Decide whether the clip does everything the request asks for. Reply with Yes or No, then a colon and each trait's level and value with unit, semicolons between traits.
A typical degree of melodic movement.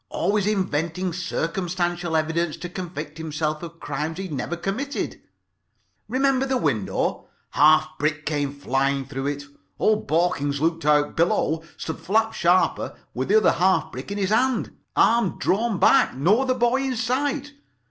No: wide, 6.1 semitones